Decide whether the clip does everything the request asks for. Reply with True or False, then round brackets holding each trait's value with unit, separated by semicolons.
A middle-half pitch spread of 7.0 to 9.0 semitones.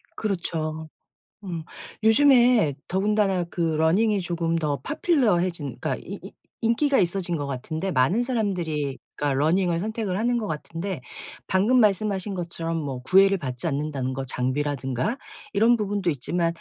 False (5.4 semitones)